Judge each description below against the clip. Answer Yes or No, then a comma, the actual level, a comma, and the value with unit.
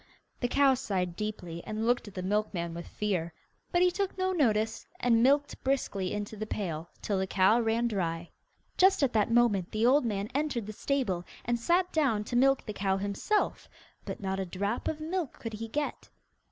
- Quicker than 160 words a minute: Yes, average, 195 wpm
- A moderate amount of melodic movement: No, wide, 5.7 semitones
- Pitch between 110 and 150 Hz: No, high, 220 Hz